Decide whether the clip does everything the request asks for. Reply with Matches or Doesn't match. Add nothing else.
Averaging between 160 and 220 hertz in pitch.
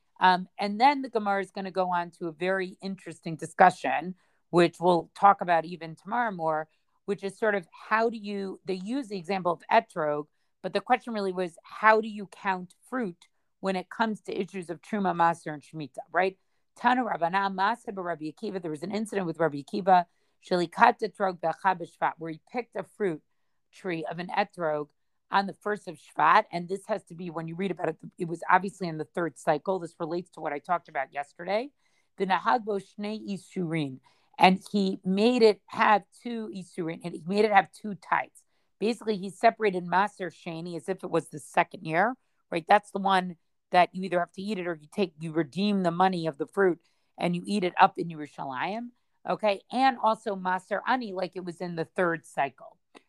Matches